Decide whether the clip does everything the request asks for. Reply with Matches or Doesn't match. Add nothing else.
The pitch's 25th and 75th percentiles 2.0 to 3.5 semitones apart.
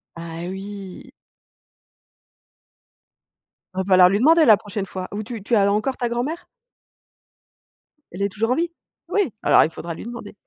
Doesn't match